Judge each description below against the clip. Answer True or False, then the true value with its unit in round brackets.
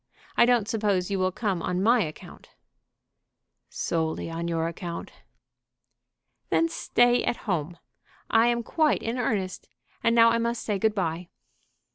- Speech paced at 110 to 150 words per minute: True (145 wpm)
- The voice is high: True (205 Hz)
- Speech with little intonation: False (5.1 semitones)